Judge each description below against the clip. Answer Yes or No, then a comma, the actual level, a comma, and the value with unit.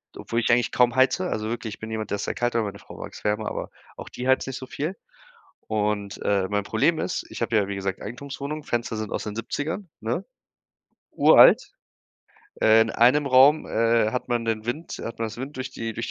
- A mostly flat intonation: No, average, 3.2 semitones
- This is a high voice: No, low, 115 Hz